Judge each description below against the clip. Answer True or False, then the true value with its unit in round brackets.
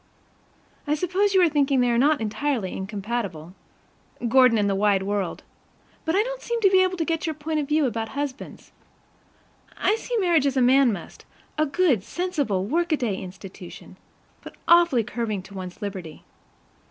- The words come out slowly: False (165 wpm)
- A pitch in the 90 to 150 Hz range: False (265 Hz)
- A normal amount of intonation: False (8.1 semitones)